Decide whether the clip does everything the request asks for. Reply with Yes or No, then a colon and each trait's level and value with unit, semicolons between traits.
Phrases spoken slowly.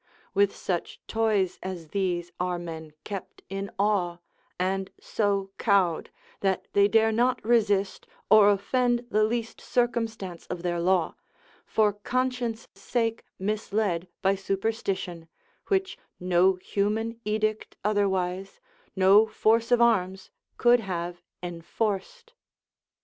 Yes: slow, 115 wpm